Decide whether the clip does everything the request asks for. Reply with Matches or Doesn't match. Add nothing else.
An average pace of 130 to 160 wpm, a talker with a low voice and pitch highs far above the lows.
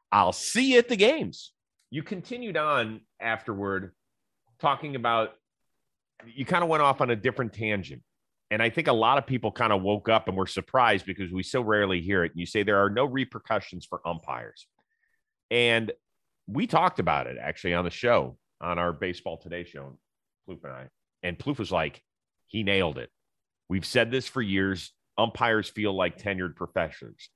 Doesn't match